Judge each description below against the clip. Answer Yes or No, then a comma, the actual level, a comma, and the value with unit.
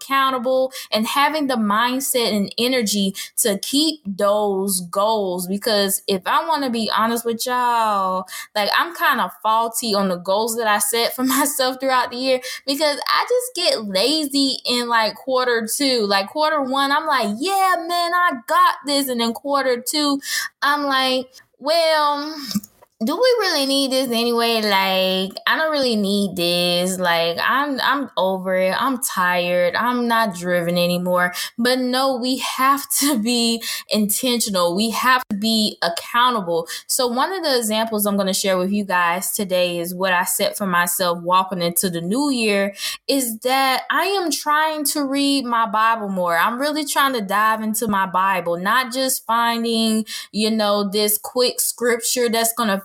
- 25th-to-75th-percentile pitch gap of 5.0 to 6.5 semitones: Yes, wide, 5.5 semitones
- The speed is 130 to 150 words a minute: No, average, 170 wpm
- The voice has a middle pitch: No, high, 235 Hz